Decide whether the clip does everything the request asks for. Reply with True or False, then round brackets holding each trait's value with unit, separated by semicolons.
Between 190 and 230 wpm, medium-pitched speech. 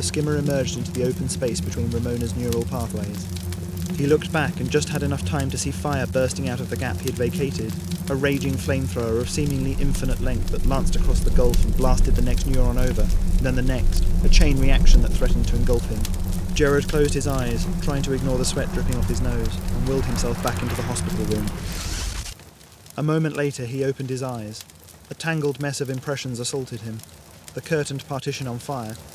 False (205 wpm; 110 Hz)